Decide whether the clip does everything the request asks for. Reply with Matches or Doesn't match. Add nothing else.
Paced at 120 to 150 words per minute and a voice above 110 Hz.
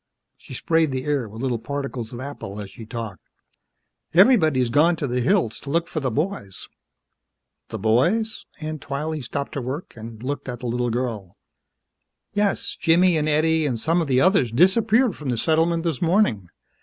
Doesn't match